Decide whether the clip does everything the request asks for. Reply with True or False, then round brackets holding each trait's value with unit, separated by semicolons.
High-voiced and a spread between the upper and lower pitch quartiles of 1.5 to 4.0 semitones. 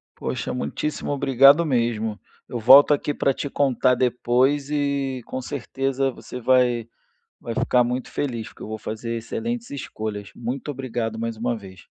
False (125 Hz; 3.0 semitones)